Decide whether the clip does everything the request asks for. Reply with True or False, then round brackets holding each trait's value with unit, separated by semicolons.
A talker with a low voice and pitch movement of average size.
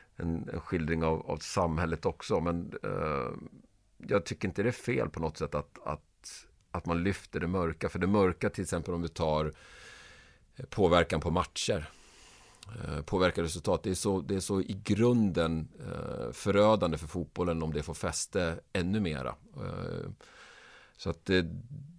True (90 Hz; 3.4 semitones)